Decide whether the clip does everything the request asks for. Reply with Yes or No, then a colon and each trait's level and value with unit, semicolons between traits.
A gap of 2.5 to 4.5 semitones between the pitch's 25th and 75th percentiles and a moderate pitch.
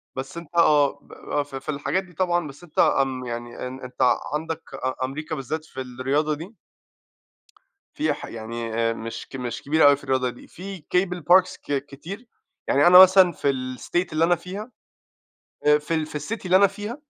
No: average, 5.2 semitones; medium, 150 Hz